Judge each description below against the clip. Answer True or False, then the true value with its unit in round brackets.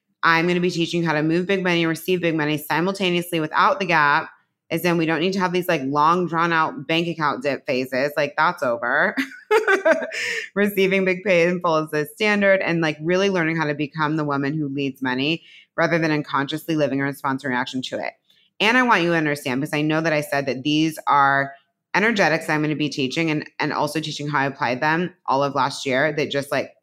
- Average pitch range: True (3.3 semitones)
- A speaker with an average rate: False (230 wpm)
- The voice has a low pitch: False (160 Hz)